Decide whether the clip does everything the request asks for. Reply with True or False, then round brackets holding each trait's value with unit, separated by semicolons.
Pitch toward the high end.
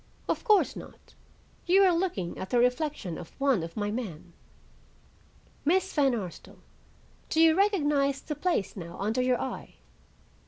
True (265 Hz)